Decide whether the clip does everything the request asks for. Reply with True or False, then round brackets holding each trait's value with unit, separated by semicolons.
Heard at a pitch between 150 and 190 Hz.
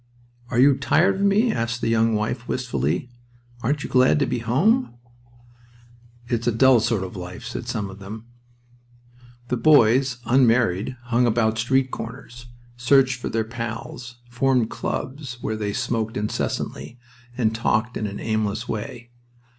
False (120 Hz)